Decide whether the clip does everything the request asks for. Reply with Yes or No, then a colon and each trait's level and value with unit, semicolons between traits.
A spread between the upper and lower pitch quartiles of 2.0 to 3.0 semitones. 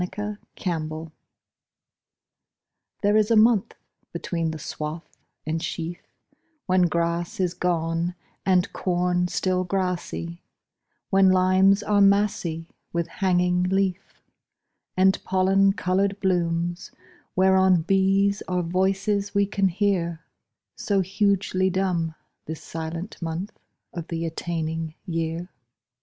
Yes: narrow, 2.4 semitones